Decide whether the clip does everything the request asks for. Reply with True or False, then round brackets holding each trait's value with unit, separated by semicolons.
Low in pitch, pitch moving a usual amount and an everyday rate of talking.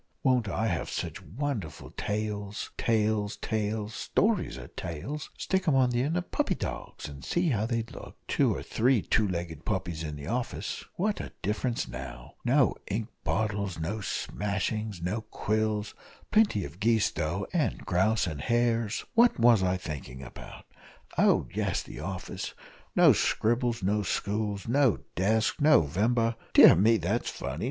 True (110 Hz; 4.2 semitones; 160 wpm)